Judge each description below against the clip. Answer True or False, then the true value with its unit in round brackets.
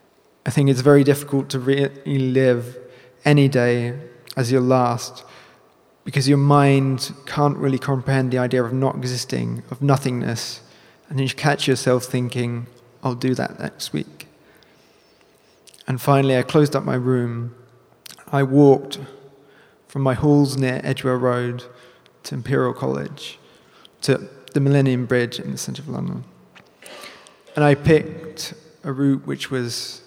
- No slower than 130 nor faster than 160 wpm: True (140 wpm)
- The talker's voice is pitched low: True (130 Hz)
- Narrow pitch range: True (2.0 semitones)